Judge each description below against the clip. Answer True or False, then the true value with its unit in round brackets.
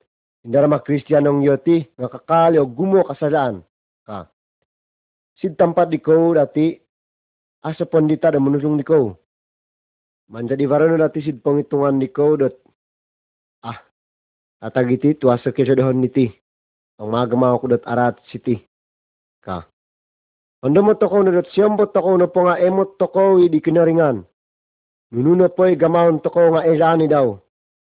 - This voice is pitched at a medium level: True (150 Hz)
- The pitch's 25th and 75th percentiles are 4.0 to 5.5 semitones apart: True (5.2 semitones)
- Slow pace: False (140 wpm)